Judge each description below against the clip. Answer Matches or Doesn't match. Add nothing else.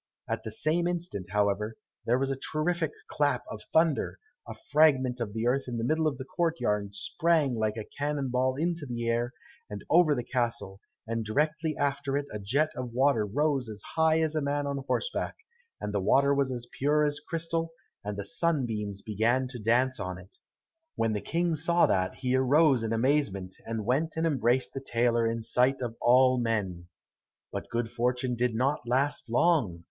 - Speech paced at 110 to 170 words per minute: Doesn't match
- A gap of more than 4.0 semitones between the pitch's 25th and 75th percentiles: Matches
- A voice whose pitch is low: Matches